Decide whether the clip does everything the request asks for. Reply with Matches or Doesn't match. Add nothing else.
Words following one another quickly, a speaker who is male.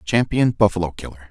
Doesn't match